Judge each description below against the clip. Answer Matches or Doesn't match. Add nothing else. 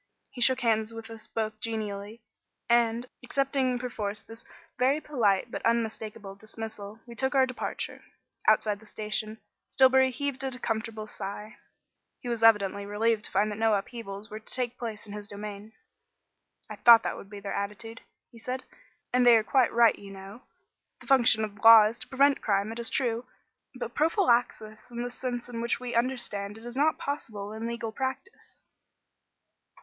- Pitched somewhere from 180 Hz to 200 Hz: Doesn't match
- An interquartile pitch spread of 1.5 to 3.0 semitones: Matches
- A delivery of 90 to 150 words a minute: Doesn't match